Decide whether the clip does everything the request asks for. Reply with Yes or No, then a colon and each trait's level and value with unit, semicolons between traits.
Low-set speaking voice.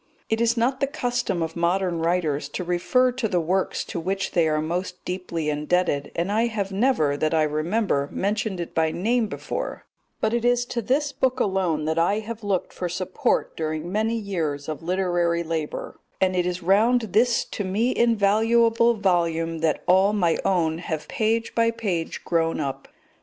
No: medium, 185 Hz